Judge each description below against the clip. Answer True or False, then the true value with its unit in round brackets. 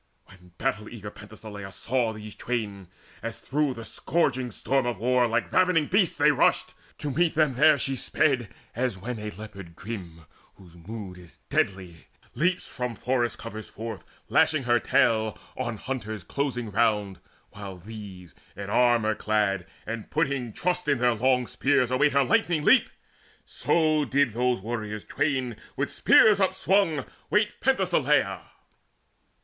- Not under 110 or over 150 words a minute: True (145 wpm)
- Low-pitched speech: True (120 Hz)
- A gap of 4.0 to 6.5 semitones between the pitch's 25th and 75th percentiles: True (5.2 semitones)